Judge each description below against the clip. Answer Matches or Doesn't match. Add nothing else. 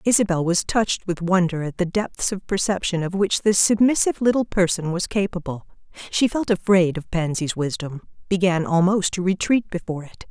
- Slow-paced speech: Doesn't match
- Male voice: Doesn't match